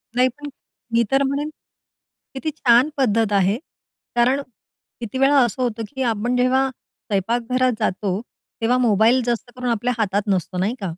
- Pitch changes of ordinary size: Yes, average, 3.4 semitones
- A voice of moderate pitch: No, high, 240 Hz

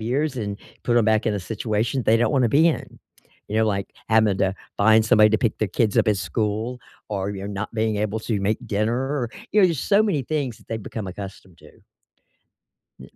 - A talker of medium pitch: No, low, 110 Hz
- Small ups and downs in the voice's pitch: No, average, 3.0 semitones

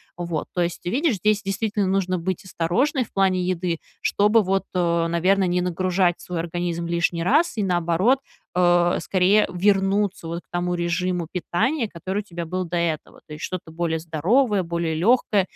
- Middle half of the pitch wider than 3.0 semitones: No, narrow, 2.4 semitones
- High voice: No, medium, 180 Hz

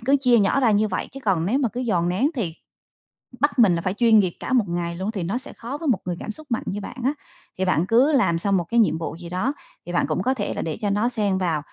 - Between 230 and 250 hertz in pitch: No, high, 210 Hz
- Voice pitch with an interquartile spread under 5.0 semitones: No, wide, 5.4 semitones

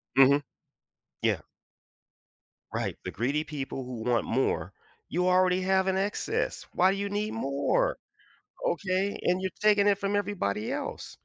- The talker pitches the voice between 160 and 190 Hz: Yes, medium, 185 Hz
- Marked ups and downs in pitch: Yes, wide, 6.4 semitones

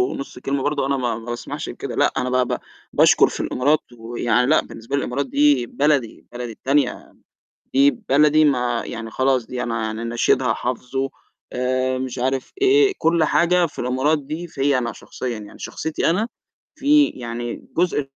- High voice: No, low, 130 Hz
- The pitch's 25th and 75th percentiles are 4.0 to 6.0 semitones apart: No, average, 3.4 semitones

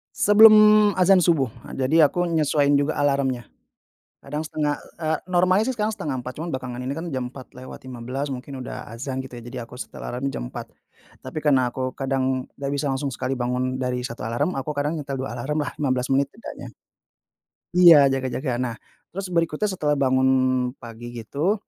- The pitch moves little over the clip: No, average, 3.6 semitones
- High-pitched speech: No, low, 135 Hz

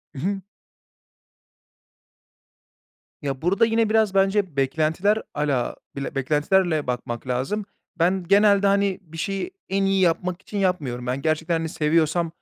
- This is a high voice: No, medium, 175 Hz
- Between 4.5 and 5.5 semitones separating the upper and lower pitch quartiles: Yes, average, 4.9 semitones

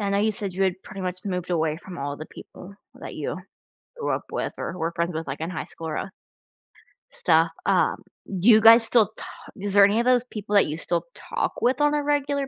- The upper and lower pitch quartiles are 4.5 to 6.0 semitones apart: Yes, average, 5.0 semitones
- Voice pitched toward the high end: Yes, high, 195 Hz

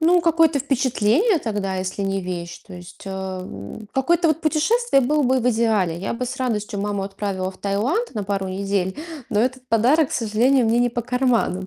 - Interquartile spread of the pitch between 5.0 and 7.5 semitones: Yes, wide, 5.5 semitones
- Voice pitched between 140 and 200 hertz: No, high, 225 Hz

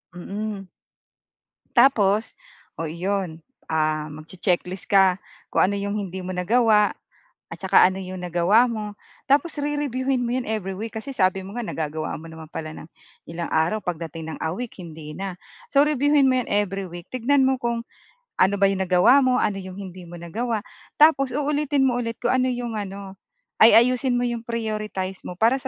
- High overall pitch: Yes, high, 205 Hz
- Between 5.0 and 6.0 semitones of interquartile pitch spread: Yes, average, 5.3 semitones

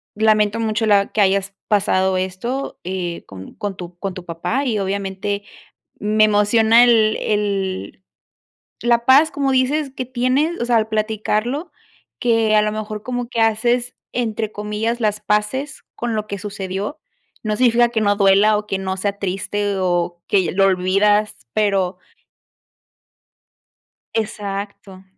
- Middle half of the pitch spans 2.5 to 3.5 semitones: Yes, average, 2.9 semitones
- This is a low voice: No, high, 210 Hz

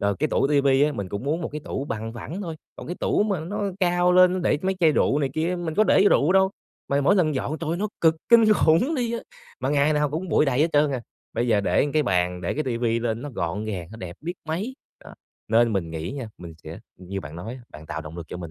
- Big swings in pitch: Yes, wide, 8.0 semitones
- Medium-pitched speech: Yes, medium, 145 Hz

